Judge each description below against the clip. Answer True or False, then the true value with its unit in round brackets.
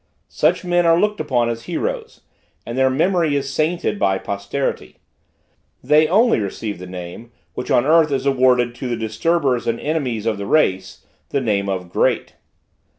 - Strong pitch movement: True (6.3 semitones)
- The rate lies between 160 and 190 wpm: True (170 wpm)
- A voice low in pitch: True (130 Hz)